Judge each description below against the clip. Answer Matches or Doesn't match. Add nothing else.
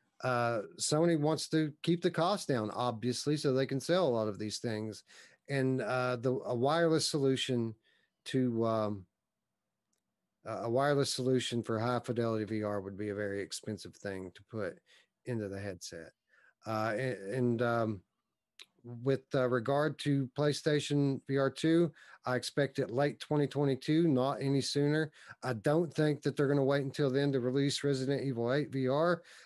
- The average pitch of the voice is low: Matches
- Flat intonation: Doesn't match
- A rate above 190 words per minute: Doesn't match